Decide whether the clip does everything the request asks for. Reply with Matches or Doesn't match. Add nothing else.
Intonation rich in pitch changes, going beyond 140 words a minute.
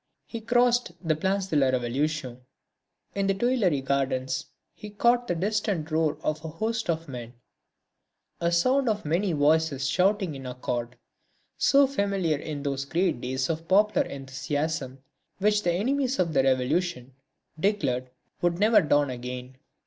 Matches